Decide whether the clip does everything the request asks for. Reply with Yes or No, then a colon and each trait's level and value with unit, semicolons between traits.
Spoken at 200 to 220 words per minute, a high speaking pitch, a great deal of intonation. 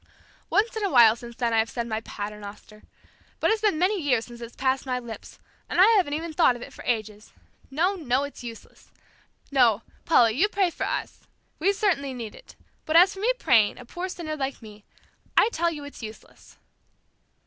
Yes: fast, 205 wpm; very high, 265 Hz; wide, 7.2 semitones